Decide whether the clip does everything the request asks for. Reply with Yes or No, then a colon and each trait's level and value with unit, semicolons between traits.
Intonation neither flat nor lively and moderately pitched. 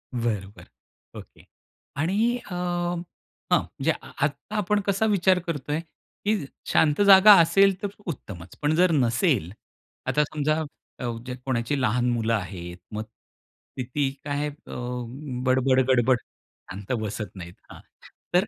No: wide, 7.0 semitones; medium, 145 Hz